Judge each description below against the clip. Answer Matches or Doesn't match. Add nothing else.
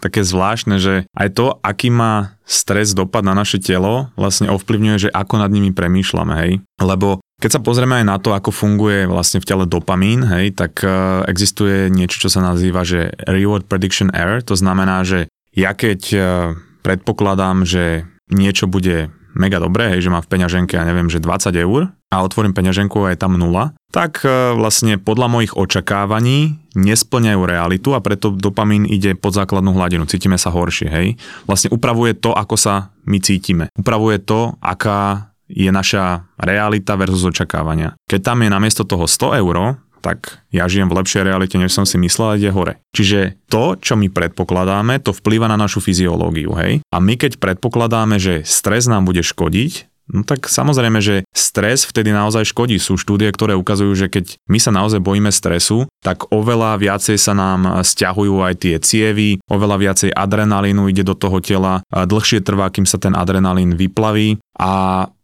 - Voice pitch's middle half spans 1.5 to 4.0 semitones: Matches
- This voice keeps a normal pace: Doesn't match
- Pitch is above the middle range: Doesn't match